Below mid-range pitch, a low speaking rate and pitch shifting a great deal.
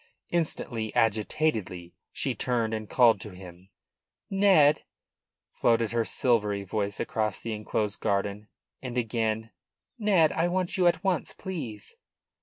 Yes: low, 115 Hz; slow, 125 wpm; wide, 6.8 semitones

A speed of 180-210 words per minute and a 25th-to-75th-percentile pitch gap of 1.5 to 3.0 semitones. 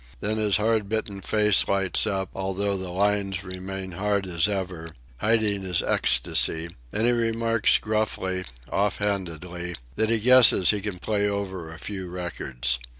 No: average, 150 wpm; narrow, 2.6 semitones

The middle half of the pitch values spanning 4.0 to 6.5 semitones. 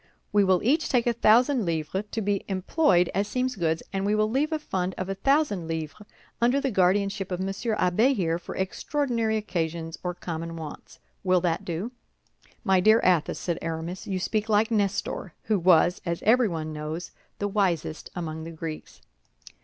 Yes: average, 4.4 semitones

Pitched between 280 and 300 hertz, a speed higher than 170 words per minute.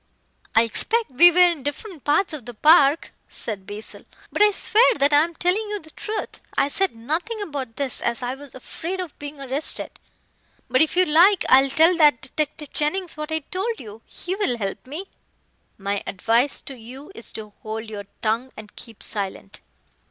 Yes: very high, 290 Hz; average, 190 wpm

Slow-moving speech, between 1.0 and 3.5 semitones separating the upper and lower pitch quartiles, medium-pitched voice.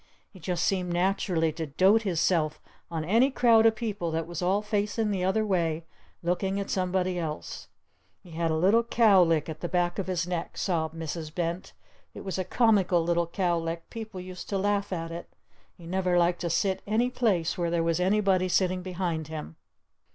No: average, 190 wpm; average, 2.9 semitones; medium, 180 Hz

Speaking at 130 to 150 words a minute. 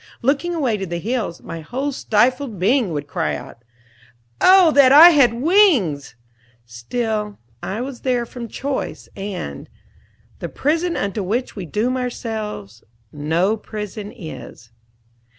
Yes: slow, 135 wpm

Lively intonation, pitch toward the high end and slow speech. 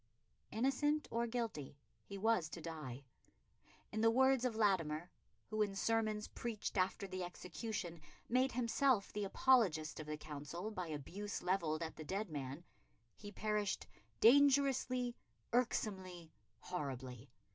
Yes: wide, 6.1 semitones; high, 200 Hz; slow, 130 wpm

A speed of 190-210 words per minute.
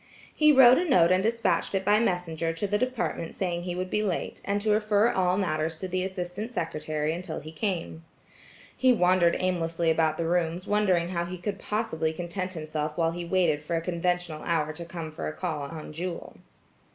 Yes: average, 200 wpm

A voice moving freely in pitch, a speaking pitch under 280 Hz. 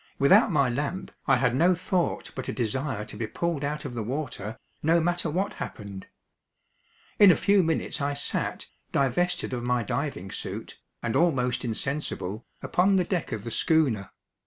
Yes: wide, 6.1 semitones; medium, 140 Hz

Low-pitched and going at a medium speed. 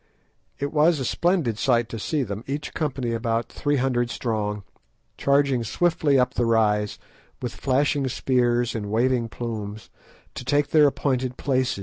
Yes: low, 125 Hz; average, 150 wpm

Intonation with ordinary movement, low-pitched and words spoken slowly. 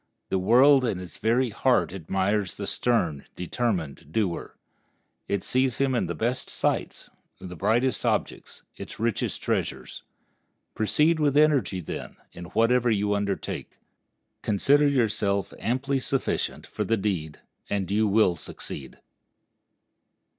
Yes: average, 4.8 semitones; low, 110 Hz; slow, 125 wpm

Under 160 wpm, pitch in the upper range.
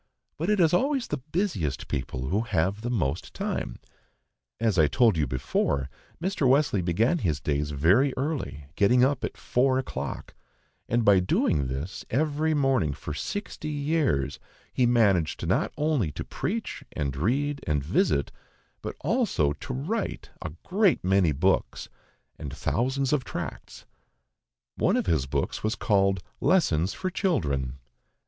No: average, 145 wpm; low, 110 Hz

